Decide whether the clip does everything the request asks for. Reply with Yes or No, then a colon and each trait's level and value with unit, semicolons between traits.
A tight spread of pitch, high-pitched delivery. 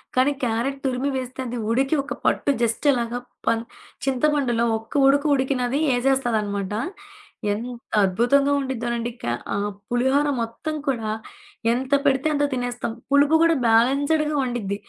No: average, 3.1 semitones; very high, 255 Hz